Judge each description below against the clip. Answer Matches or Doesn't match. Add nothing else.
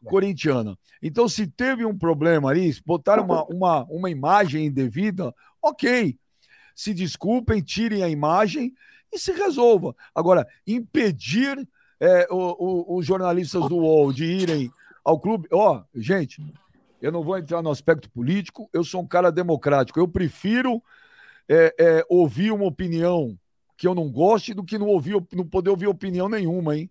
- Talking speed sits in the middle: Matches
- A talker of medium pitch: Matches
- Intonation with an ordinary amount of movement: Matches